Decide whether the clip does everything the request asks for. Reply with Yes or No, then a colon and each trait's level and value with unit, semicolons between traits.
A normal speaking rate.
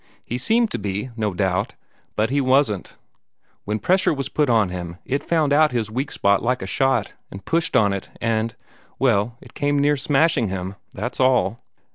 Yes: average, 185 wpm